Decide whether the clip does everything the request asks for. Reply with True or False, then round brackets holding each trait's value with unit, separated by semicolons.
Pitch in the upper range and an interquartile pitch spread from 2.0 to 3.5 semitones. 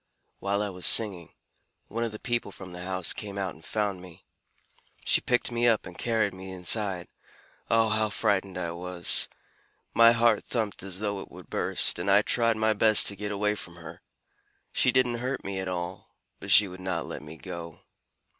False (100 Hz; 3.2 semitones)